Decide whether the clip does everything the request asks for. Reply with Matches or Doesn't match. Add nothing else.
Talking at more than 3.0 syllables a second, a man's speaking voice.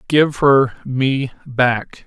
Doesn't match